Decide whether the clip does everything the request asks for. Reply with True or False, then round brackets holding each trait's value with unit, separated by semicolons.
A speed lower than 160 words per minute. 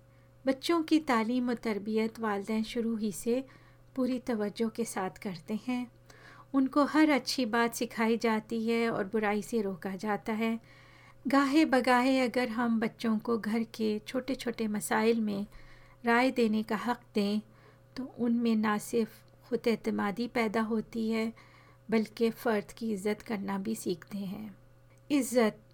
True (145 wpm)